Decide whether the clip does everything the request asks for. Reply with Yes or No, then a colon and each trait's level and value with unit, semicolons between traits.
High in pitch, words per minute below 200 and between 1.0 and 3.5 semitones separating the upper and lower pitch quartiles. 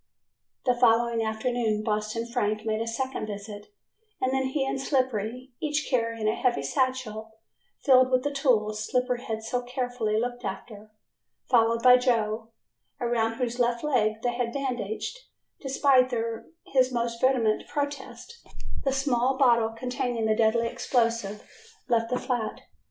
Yes: high, 240 Hz; average, 140 wpm; narrow, 2.6 semitones